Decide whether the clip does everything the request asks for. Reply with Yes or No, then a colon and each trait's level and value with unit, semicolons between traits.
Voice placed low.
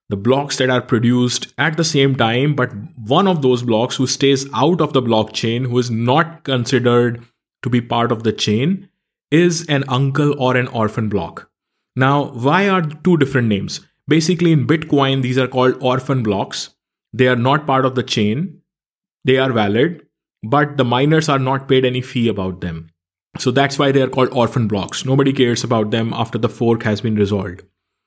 Yes: low, 130 Hz